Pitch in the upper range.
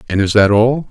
No: low, 110 Hz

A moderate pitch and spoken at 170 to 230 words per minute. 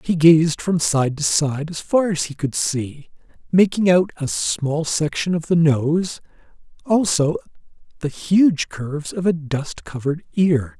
No: medium, 160 Hz; average, 160 wpm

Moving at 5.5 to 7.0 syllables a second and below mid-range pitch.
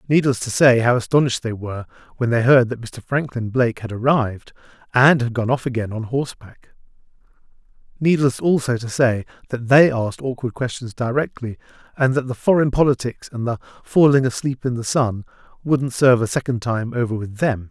Yes: 5.6 syllables/s; low, 125 Hz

